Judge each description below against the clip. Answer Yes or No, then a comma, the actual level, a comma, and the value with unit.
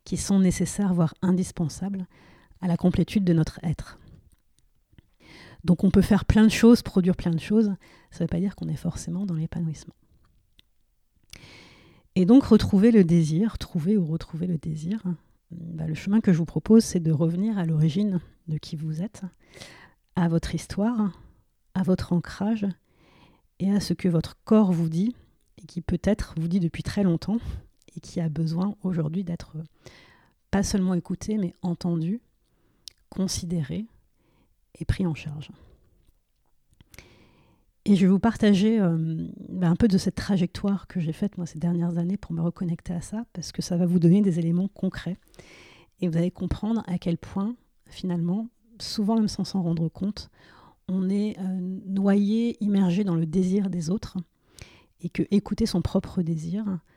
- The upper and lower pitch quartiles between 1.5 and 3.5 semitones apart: Yes, average, 3.0 semitones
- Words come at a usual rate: Yes, average, 165 wpm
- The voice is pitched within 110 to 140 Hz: No, medium, 180 Hz